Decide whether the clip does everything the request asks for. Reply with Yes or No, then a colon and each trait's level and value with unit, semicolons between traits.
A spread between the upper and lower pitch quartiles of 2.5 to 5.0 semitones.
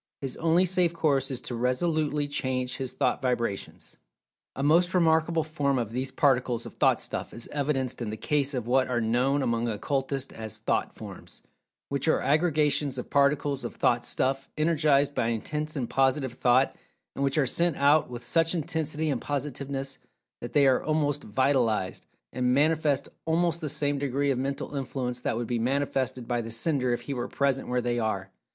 Yes: average, 3.2 semitones